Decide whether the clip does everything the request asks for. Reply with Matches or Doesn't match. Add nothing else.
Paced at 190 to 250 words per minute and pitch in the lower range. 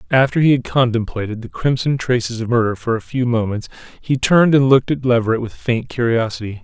Matches